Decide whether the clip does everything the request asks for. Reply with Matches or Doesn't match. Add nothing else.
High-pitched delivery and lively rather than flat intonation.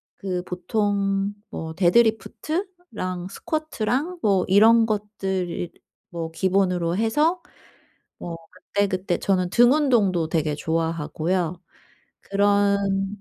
Doesn't match